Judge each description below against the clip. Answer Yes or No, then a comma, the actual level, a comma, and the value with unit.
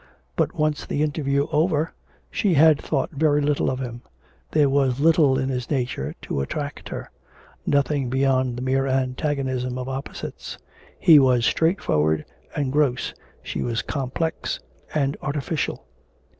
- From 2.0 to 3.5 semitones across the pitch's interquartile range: Yes, average, 2.7 semitones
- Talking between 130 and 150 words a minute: Yes, average, 140 wpm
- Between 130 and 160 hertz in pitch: Yes, medium, 140 Hz